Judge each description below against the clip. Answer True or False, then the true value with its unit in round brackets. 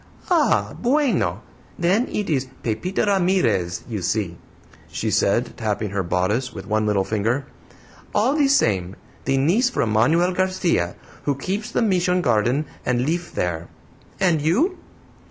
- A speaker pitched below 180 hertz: True (140 Hz)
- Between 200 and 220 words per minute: False (140 wpm)